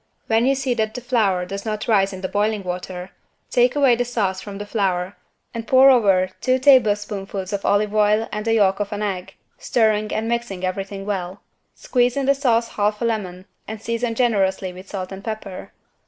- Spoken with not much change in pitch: No, average, 3.2 semitones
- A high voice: Yes, high, 210 Hz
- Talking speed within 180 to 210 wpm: Yes, average, 200 wpm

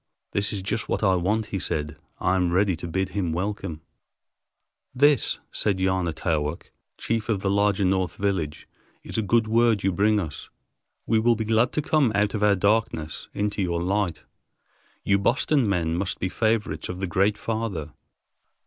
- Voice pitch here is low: Yes, low, 100 Hz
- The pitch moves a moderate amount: Yes, average, 3.4 semitones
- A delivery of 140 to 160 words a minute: No, average, 175 wpm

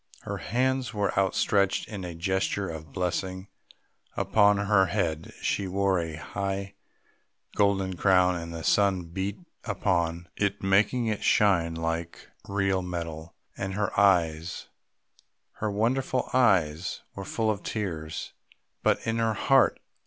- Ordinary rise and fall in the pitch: Yes, average, 3.1 semitones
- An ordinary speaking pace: No, slow, 130 wpm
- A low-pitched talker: Yes, very low, 95 Hz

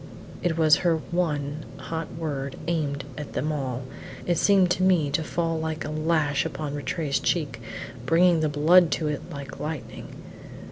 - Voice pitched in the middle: Yes, medium, 155 Hz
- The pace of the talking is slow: No, average, 160 wpm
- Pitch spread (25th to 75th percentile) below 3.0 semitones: Yes, narrow, 2.4 semitones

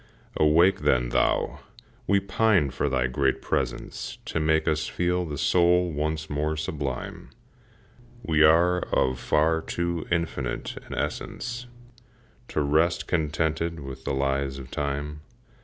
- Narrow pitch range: No, average, 3.5 semitones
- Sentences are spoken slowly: Yes, slow, 130 wpm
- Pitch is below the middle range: Yes, very low, 75 Hz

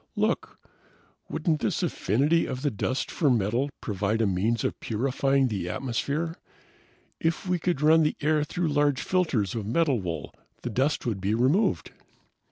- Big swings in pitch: Yes, wide, 5.9 semitones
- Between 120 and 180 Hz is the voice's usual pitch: Yes, low, 135 Hz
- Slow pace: No, average, 160 wpm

